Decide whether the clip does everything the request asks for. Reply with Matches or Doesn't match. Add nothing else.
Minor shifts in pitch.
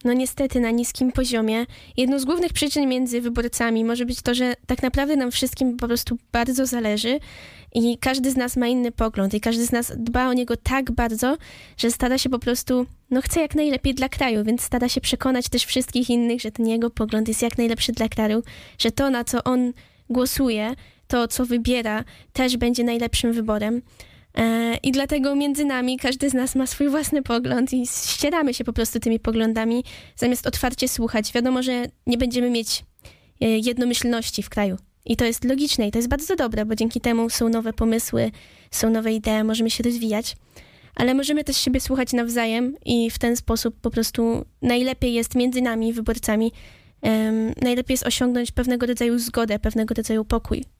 Matches